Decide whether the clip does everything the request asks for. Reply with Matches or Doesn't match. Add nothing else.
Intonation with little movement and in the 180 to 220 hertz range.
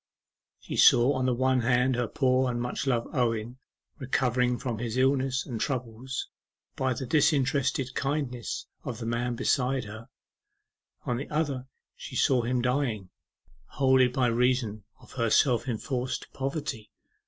Doesn't match